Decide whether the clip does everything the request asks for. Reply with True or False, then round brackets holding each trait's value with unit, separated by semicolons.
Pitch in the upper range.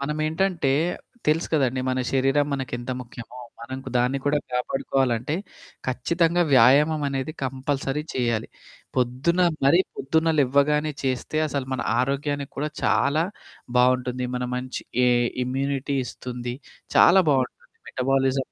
False (135 Hz)